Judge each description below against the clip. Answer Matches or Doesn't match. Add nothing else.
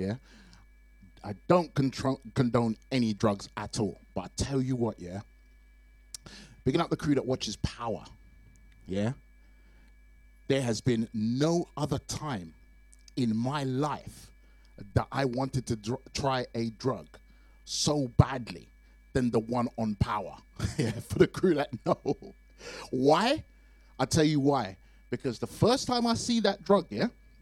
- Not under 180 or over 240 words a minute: Doesn't match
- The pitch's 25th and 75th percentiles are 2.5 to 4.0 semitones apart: Doesn't match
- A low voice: Matches